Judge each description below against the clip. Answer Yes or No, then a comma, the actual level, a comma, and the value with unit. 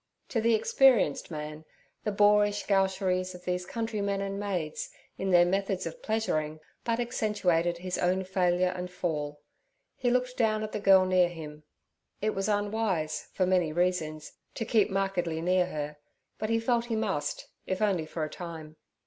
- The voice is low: No, medium, 185 Hz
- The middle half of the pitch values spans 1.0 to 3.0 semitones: No, average, 3.6 semitones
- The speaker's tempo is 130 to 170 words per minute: Yes, average, 165 wpm